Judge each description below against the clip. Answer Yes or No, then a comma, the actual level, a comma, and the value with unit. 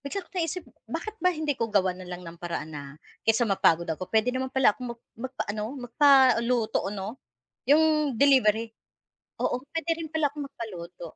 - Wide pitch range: Yes, wide, 6.3 semitones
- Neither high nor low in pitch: No, high, 245 Hz